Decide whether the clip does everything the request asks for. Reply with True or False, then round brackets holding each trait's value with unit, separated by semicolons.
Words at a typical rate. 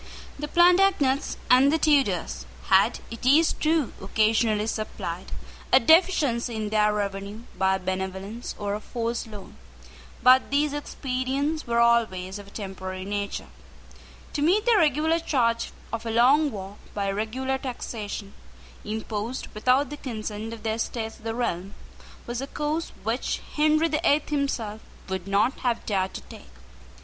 True (150 wpm)